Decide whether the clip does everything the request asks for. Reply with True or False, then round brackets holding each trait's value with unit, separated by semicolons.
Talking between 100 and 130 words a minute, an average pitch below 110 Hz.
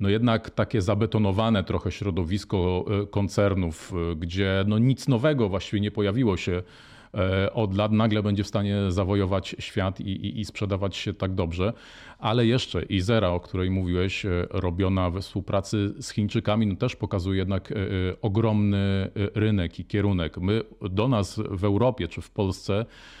False (145 wpm; 100 Hz)